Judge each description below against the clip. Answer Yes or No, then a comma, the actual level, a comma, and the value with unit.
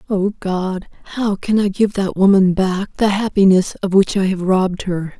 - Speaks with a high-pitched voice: Yes, high, 195 Hz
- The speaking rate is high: No, average, 195 wpm